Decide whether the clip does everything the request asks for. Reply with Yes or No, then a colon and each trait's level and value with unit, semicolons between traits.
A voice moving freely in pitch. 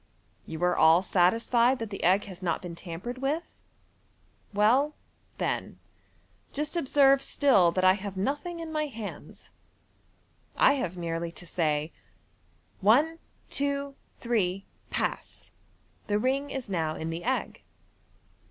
Yes: wide, 7.5 semitones